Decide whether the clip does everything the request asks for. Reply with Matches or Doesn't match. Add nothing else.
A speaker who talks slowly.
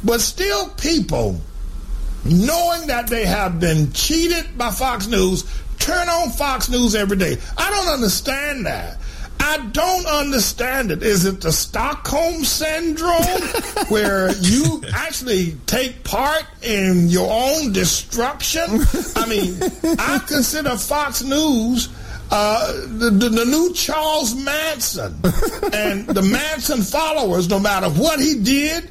Matches